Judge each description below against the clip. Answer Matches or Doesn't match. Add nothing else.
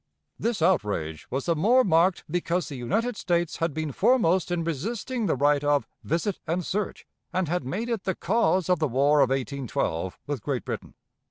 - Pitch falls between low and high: Matches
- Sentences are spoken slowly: Doesn't match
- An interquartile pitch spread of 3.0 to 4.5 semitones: Doesn't match